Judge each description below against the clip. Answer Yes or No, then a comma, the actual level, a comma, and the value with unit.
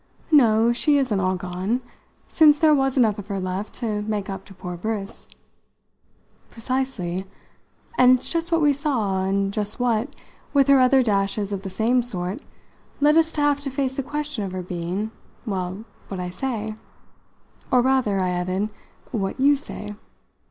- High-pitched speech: Yes, high, 220 Hz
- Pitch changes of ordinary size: No, wide, 5.7 semitones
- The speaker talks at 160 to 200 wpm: Yes, average, 170 wpm